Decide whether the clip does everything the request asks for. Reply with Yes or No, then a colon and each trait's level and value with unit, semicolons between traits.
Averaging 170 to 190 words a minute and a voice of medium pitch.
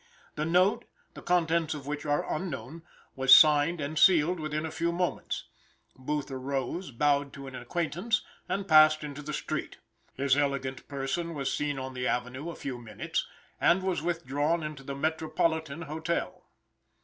No: average, 160 wpm; medium, 150 Hz